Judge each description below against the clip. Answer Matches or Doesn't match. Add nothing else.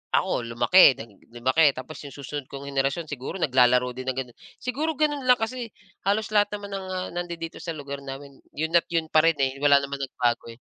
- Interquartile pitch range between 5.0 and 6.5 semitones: Matches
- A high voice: Doesn't match